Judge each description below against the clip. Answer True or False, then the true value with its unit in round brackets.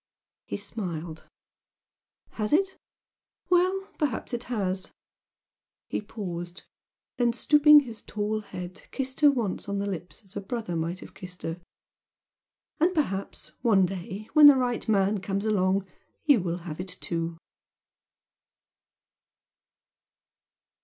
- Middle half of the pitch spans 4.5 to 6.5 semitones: True (5.2 semitones)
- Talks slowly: True (125 wpm)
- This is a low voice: False (205 Hz)